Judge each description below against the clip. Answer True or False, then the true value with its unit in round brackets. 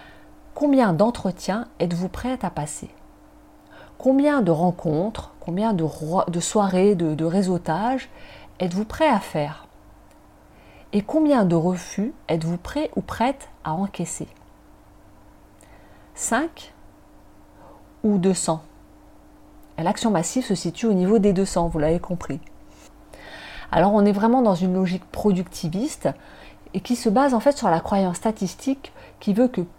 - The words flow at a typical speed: False (130 wpm)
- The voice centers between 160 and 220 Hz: True (190 Hz)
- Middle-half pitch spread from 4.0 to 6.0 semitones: True (5.4 semitones)